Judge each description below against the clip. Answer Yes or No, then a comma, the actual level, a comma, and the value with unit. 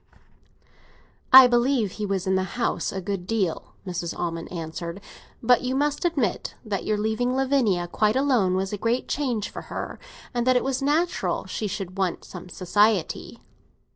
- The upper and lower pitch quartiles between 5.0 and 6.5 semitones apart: Yes, average, 5.3 semitones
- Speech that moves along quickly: No, average, 170 wpm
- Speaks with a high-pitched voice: Yes, high, 215 Hz